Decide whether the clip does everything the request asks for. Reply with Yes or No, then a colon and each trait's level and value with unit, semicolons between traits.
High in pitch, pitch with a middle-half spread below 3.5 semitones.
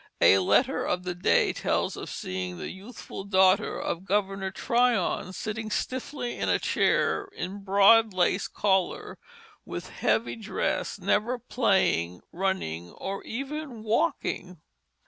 No: high, 195 Hz; average, 3.9 semitones